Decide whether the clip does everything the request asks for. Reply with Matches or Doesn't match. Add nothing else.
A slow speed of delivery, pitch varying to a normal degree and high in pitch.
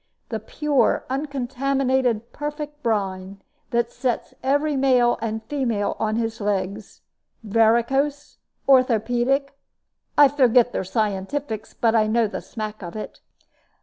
Matches